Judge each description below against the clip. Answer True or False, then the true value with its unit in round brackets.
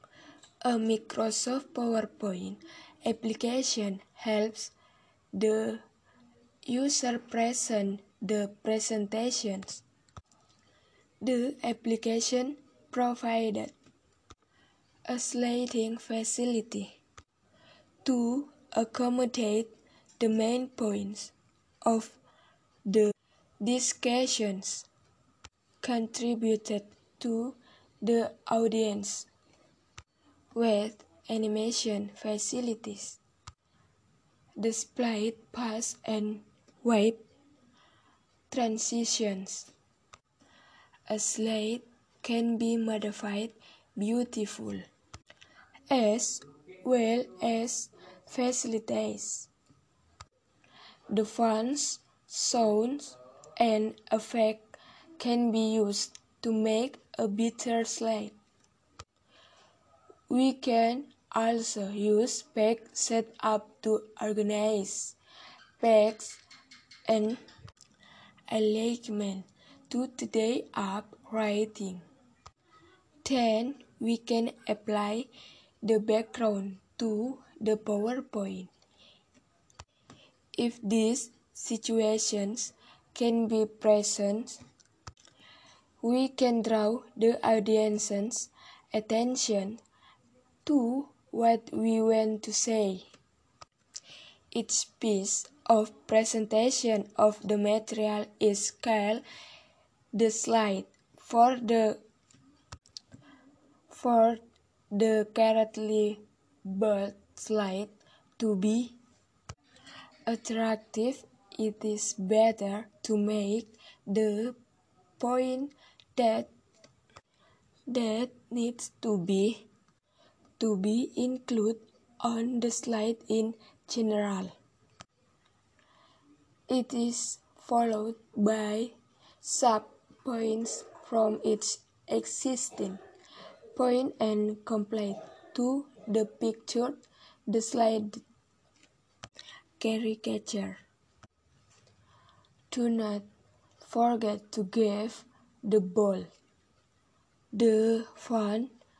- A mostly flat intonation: True (2.0 semitones)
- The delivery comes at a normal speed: False (70 wpm)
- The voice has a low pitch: False (225 Hz)